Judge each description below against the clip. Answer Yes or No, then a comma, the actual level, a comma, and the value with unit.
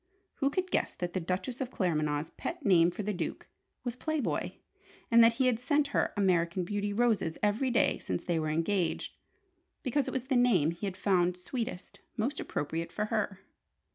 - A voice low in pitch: No, high, 205 Hz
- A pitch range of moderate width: No, wide, 6.0 semitones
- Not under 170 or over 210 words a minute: Yes, average, 190 wpm